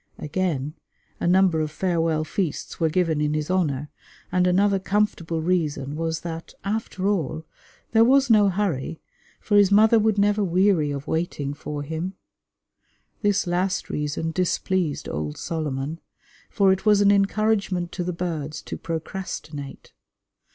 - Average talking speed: Yes, average, 145 wpm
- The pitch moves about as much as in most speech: Yes, average, 4.2 semitones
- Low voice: No, medium, 175 Hz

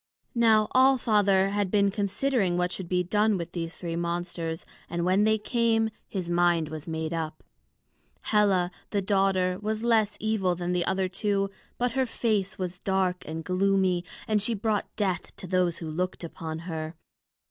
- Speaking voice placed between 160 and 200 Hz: Yes, high, 190 Hz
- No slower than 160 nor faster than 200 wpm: Yes, average, 170 wpm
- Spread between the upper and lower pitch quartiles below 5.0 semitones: Yes, average, 3.2 semitones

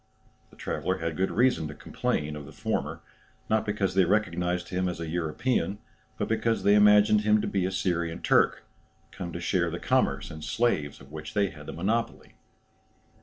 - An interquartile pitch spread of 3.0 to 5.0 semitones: Yes, average, 4.1 semitones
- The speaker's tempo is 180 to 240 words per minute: Yes, average, 185 wpm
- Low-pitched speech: Yes, very low, 90 Hz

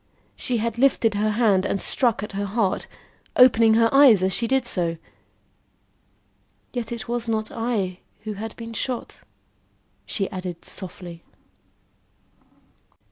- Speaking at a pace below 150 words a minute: Yes, slow, 135 wpm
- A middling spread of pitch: Yes, average, 3.3 semitones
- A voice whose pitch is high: Yes, high, 220 Hz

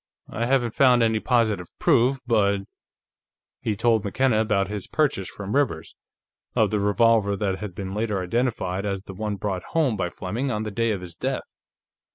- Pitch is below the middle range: Yes, low, 105 Hz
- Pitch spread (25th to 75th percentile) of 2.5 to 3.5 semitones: Yes, average, 3.1 semitones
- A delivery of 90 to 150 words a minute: No, average, 185 wpm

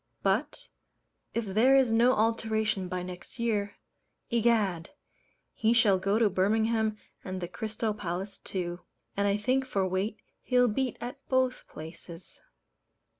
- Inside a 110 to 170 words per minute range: Yes, slow, 135 wpm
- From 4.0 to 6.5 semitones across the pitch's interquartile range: No, average, 3.6 semitones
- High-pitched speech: Yes, high, 215 Hz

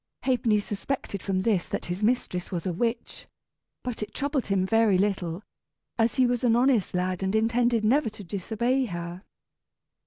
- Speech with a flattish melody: No, average, 4.3 semitones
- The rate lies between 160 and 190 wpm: Yes, average, 165 wpm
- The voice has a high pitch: Yes, high, 215 Hz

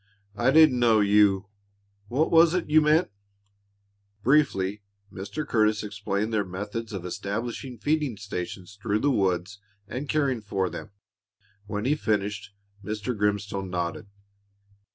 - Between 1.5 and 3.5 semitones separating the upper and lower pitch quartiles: No, average, 4.4 semitones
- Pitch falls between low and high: No, low, 105 Hz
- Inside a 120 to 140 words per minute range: Yes, slow, 135 wpm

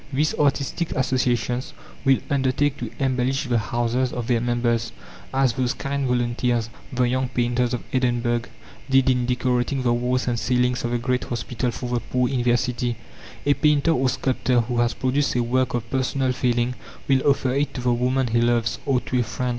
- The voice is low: Yes, low, 125 Hz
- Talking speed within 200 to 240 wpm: No, average, 190 wpm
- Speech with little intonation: Yes, narrow, 1.6 semitones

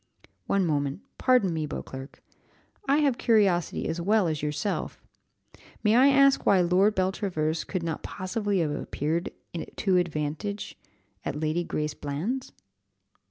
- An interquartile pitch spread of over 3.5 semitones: Yes, average, 5.3 semitones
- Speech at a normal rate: No, slow, 130 wpm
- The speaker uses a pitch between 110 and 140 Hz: No, medium, 180 Hz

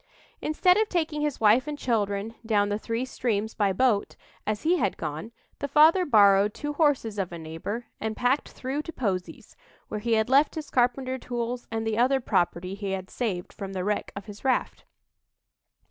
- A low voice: No, high, 225 Hz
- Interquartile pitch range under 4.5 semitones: No, average, 4.9 semitones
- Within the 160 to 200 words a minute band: Yes, average, 190 wpm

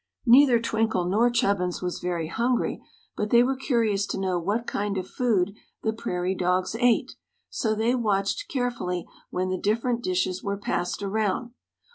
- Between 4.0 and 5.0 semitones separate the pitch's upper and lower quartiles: Yes, average, 4.3 semitones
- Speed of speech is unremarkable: Yes, average, 160 wpm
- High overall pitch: Yes, high, 210 Hz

